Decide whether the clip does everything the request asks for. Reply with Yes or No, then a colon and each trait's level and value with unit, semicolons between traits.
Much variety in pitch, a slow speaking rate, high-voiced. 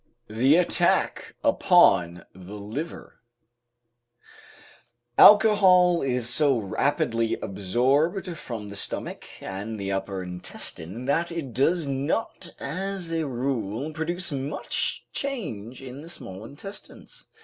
No: wide, 7.9 semitones; slow, 105 wpm; low, 135 Hz